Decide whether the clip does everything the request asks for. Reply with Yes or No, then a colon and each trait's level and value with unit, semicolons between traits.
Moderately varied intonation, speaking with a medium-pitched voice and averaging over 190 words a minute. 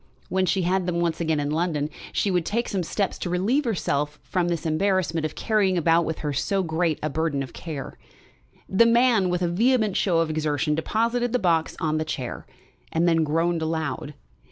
Yes: average, 3.3 semitones; medium, 170 Hz; average, 200 wpm